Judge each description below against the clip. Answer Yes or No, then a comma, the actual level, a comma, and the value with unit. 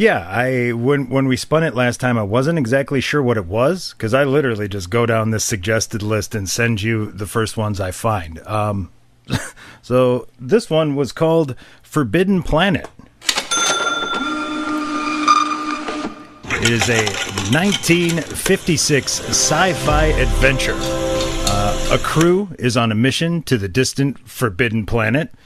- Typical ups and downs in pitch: No, wide, 6.3 semitones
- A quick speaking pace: No, average, 140 wpm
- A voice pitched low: Yes, low, 125 Hz